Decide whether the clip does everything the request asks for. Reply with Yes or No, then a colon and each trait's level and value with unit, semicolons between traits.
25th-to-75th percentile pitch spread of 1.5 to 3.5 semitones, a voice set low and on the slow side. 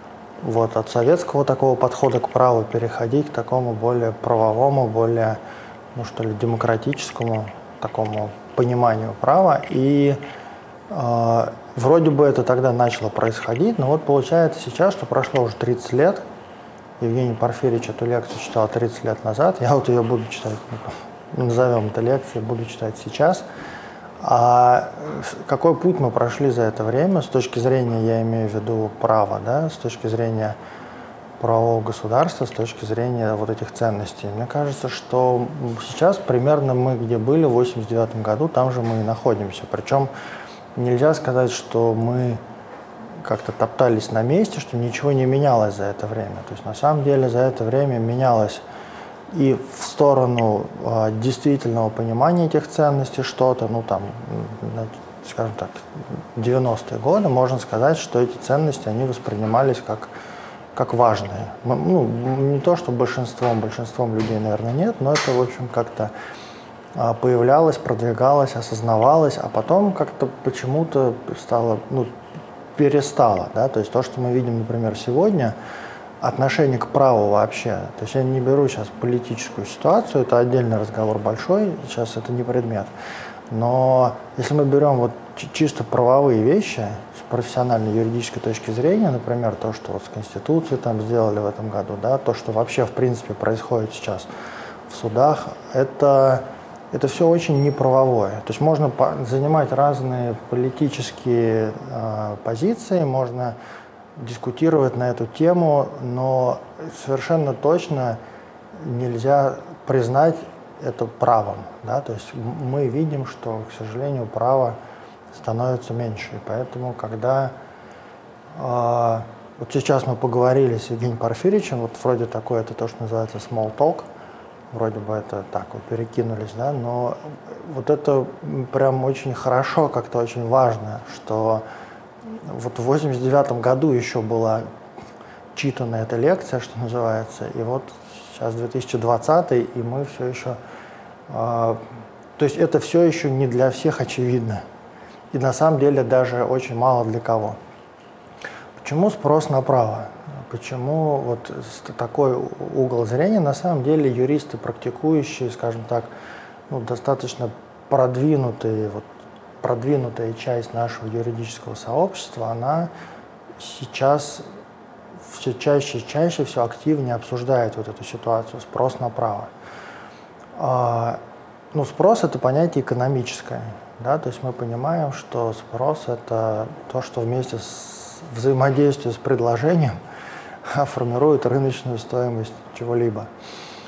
No: average, 3.0 semitones; low, 125 Hz; average, 135 wpm